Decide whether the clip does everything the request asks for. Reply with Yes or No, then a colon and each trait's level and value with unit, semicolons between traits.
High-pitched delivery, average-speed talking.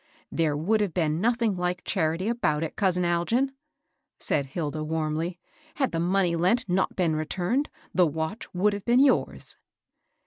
No: medium, 180 Hz; average, 170 wpm